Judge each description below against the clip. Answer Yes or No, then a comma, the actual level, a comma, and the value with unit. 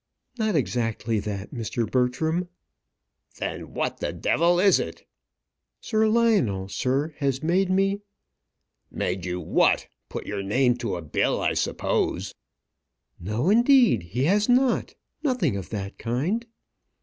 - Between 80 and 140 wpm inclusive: Yes, slow, 135 wpm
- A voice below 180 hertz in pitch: Yes, low, 135 Hz